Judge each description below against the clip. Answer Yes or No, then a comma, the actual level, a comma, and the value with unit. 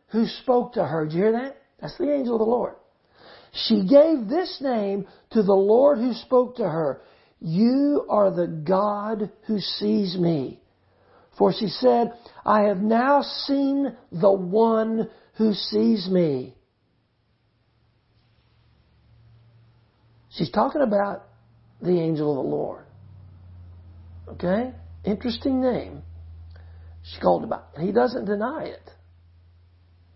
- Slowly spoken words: Yes, slow, 125 wpm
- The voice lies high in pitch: Yes, high, 195 Hz